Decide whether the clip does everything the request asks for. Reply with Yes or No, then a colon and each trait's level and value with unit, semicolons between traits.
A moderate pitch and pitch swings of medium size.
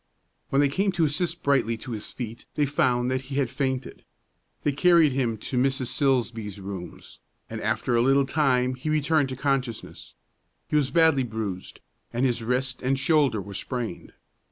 No: low, 130 Hz; average, 3.1 semitones